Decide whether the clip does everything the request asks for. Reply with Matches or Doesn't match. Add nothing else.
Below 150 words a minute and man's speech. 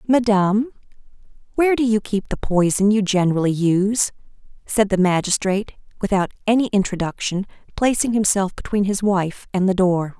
Doesn't match